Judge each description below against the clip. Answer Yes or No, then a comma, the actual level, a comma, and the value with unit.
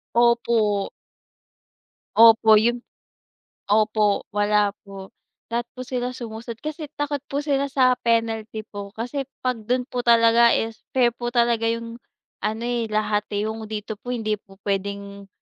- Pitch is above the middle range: Yes, high, 230 Hz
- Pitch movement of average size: No, narrow, 2.3 semitones